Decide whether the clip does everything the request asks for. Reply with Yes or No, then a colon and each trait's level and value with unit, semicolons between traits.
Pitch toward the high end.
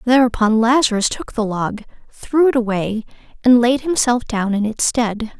Yes: high, 235 Hz